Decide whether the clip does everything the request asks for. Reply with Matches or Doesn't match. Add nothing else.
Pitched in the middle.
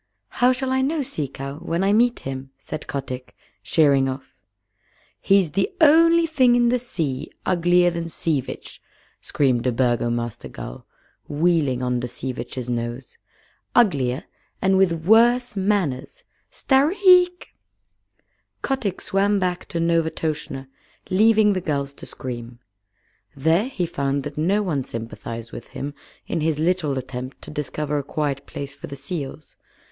Matches